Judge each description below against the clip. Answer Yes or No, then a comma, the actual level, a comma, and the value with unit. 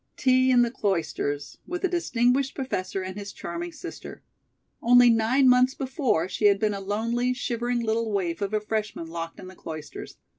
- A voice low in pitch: No, high, 230 Hz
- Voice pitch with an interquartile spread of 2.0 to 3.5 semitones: No, average, 4.6 semitones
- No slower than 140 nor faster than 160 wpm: No, average, 180 wpm